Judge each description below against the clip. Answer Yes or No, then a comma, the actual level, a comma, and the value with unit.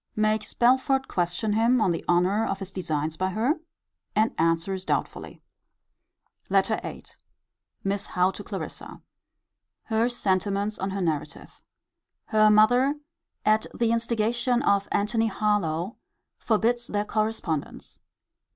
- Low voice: No, high, 210 Hz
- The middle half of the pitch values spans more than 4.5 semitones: No, average, 3.4 semitones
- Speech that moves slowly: Yes, slow, 120 wpm